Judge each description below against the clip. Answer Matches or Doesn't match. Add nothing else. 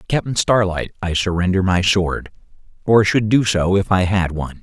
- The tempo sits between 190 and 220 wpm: Doesn't match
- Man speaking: Matches